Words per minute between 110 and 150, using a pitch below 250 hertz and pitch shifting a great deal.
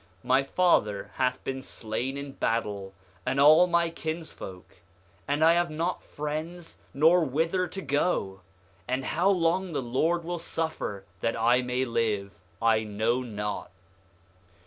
Yes: average, 140 wpm; low, 135 Hz; wide, 6.4 semitones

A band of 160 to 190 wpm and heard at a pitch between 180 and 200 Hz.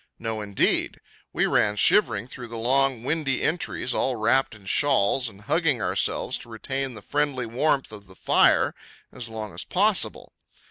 No: average, 165 wpm; low, 125 Hz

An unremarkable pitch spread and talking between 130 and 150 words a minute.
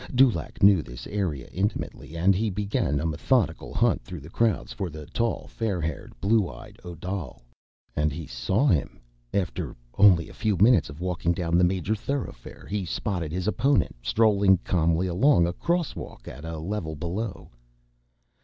No: average, 4.5 semitones; average, 165 wpm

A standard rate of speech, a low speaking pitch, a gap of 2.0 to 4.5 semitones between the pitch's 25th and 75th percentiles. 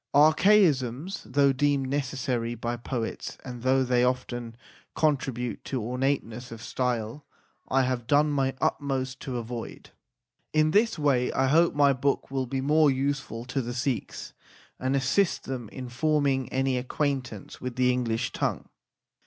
Yes: average, 145 wpm; low, 130 Hz; narrow, 2.5 semitones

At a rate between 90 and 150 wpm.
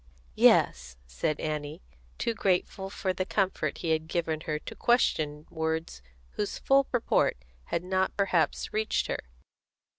Yes: average, 140 wpm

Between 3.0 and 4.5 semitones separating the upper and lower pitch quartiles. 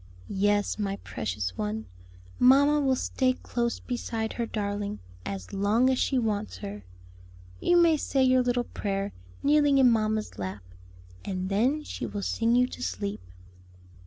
No: average, 5.2 semitones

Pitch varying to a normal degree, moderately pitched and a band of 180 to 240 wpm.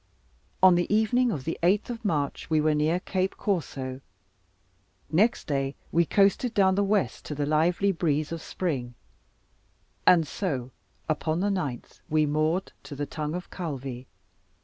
No: average, 4.6 semitones; medium, 165 Hz; average, 155 wpm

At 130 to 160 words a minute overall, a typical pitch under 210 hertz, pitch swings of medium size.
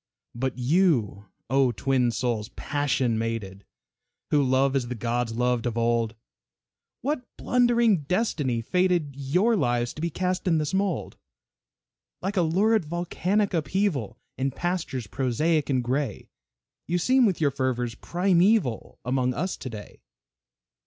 No: slow, 135 wpm; medium, 140 Hz; wide, 6.8 semitones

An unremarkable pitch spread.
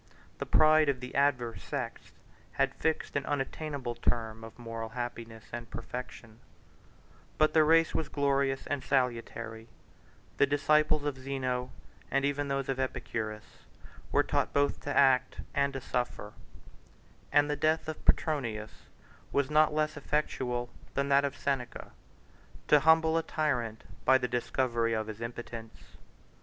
Yes: average, 3.5 semitones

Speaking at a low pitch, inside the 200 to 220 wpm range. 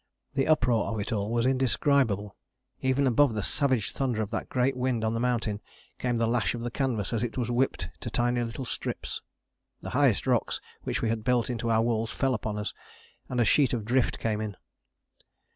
Yes: low, 120 Hz; fast, 205 wpm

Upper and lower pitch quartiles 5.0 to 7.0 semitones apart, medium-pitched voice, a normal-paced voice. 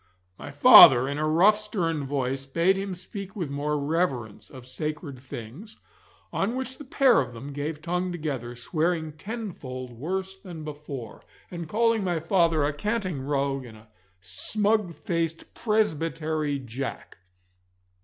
Yes: wide, 5.6 semitones; medium, 155 Hz; average, 145 wpm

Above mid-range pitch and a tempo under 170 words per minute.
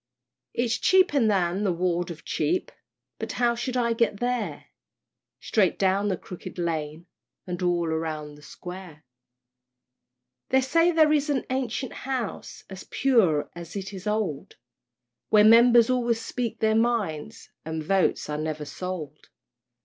Yes: high, 200 Hz; average, 140 wpm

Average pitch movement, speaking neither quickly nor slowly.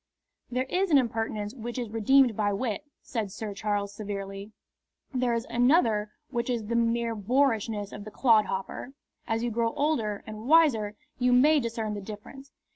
Yes: average, 3.2 semitones; average, 165 wpm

